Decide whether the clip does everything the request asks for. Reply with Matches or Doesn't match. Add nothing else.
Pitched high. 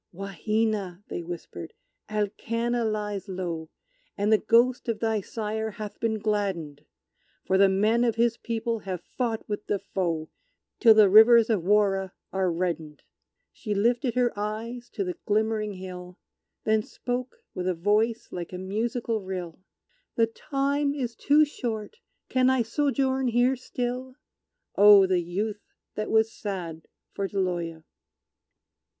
Matches